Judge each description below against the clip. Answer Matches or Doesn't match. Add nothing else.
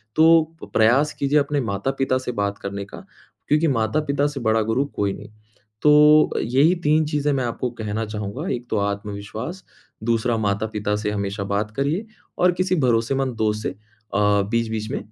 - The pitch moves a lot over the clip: Matches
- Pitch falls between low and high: Doesn't match